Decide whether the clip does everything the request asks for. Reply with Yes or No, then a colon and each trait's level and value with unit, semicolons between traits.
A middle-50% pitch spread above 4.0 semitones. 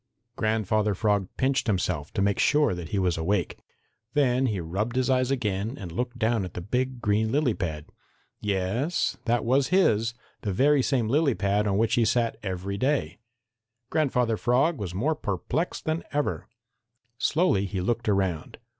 Yes: average, 5.0 semitones